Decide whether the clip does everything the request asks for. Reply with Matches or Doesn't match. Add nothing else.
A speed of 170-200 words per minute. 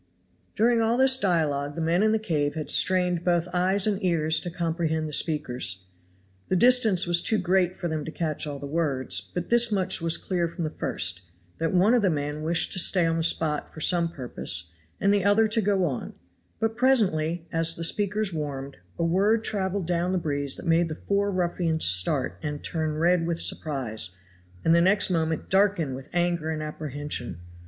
Matches